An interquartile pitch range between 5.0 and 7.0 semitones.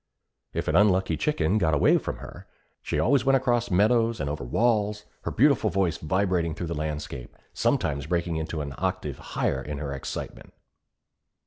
Yes: wide, 5.6 semitones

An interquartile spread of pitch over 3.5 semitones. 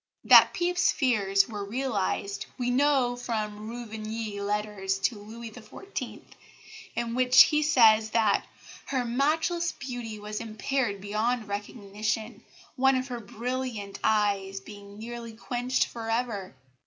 No: average, 3.2 semitones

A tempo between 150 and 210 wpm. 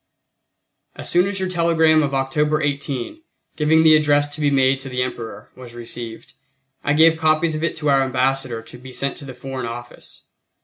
Yes: average, 190 wpm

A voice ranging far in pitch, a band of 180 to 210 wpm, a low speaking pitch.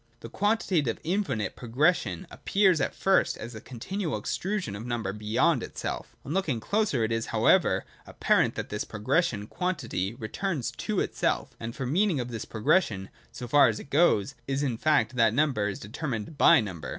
Yes: wide, 7.3 semitones; average, 185 wpm; low, 125 Hz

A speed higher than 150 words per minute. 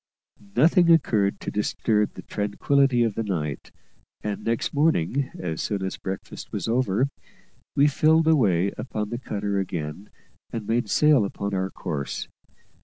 No: average, 145 wpm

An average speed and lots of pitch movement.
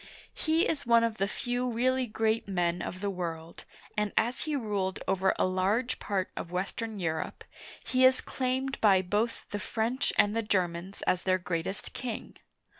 No: average, 175 wpm; average, 4.7 semitones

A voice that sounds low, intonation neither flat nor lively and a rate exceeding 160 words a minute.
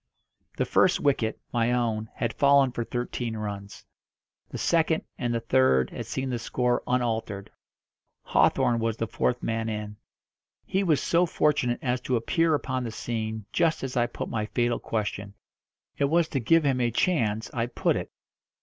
Yes: low, 120 Hz; average, 3.2 semitones; average, 170 wpm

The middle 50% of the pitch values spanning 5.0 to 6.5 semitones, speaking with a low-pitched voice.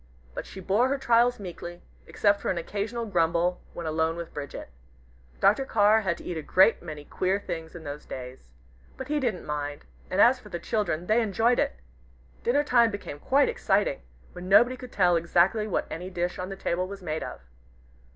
No: average, 5.3 semitones; medium, 185 Hz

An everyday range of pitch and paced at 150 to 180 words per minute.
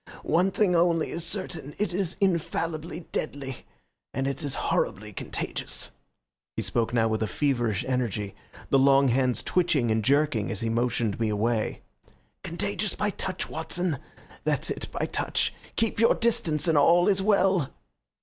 No: wide, 6.9 semitones; average, 155 wpm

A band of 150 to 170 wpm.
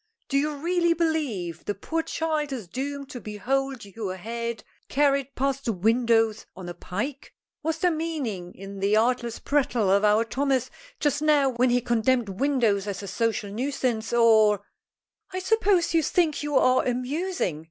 Yes: average, 165 wpm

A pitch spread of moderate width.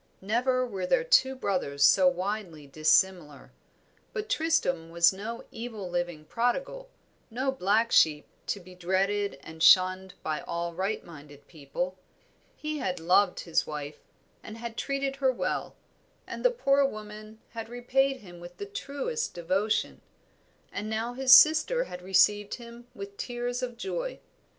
No: wide, 6.1 semitones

